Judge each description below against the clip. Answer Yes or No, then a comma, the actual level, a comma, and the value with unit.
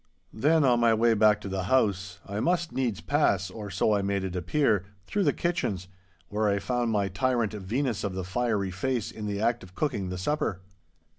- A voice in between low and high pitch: No, low, 105 Hz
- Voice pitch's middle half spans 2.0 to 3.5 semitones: No, average, 4.1 semitones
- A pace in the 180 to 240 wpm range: Yes, average, 195 wpm